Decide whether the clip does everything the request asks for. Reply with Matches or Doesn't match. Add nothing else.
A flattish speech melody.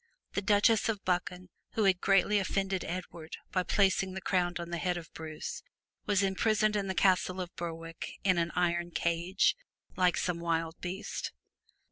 Matches